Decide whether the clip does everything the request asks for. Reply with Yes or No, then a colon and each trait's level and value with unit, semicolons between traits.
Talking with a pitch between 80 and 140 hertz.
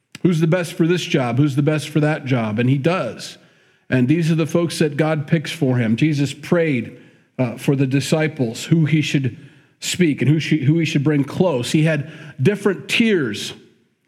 No: medium, 155 Hz